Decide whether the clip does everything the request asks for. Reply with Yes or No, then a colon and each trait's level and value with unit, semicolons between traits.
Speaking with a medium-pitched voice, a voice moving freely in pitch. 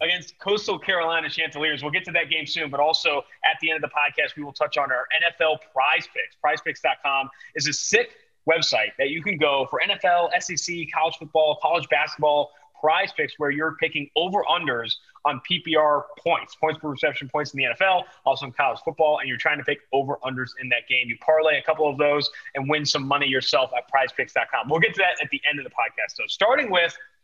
No: medium, 155 Hz; narrow, 2.5 semitones